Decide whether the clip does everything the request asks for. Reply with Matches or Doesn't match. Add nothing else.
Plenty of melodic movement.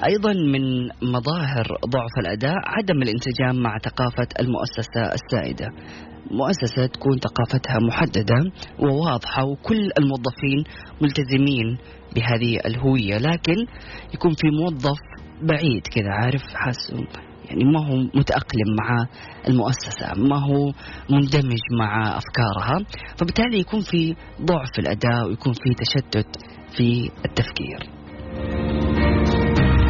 Doesn't match